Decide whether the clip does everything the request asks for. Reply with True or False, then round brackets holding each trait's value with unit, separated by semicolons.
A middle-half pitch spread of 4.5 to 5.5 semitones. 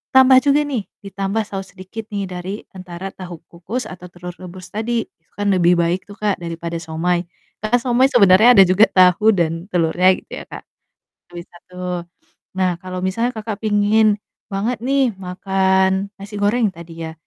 False (3.2 semitones)